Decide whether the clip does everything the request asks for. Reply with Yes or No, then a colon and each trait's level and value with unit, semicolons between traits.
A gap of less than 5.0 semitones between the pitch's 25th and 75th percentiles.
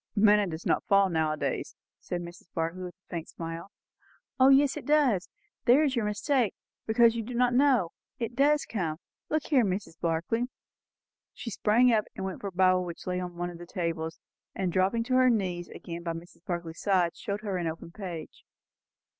No: average, 5.3 semitones